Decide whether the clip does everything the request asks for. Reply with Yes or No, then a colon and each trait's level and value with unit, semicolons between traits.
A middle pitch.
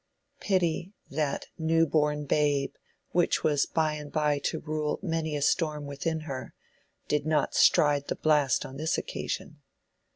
Yes: medium, 150 Hz